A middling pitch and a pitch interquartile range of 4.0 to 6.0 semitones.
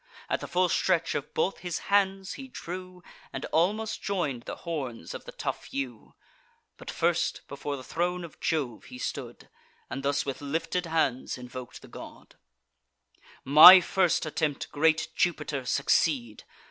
Yes: medium, 160 Hz; average, 4.7 semitones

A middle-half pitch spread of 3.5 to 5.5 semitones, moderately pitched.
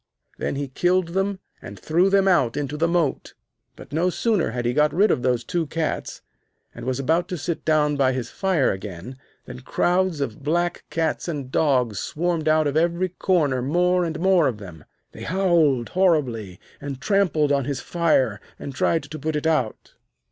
Yes: average, 5.0 semitones; medium, 155 Hz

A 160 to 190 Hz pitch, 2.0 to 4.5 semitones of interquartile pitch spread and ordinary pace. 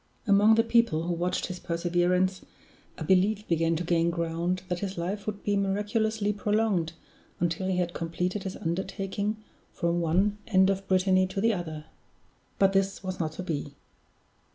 Yes: medium, 185 Hz; average, 2.9 semitones; average, 165 wpm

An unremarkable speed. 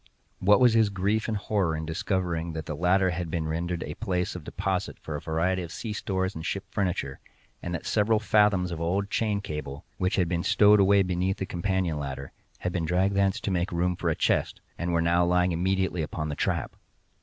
No: fast, 215 wpm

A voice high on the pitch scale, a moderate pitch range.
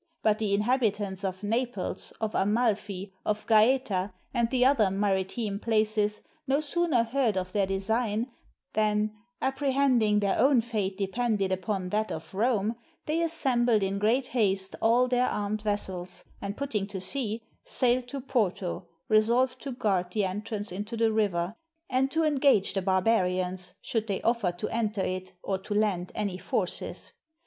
Yes: high, 215 Hz; average, 3.8 semitones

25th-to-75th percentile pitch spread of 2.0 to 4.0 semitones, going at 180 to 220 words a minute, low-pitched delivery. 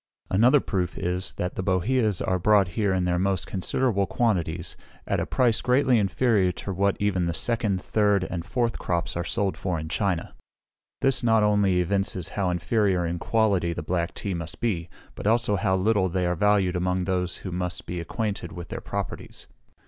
Yes: average, 3.0 semitones; average, 185 wpm; very low, 95 Hz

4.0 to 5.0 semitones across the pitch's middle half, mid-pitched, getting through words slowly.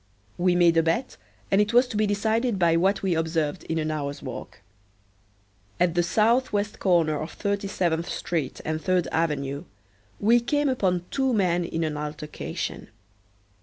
No: average, 4.3 semitones; medium, 175 Hz; average, 165 wpm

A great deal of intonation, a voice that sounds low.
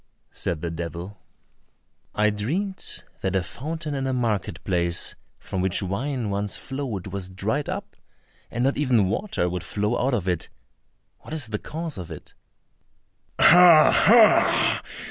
Yes: wide, 7.3 semitones; low, 105 Hz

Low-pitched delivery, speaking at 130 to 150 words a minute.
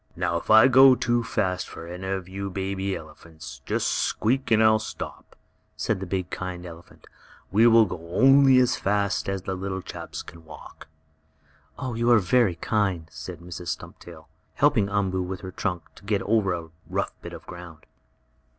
No: very low, 95 Hz; average, 175 wpm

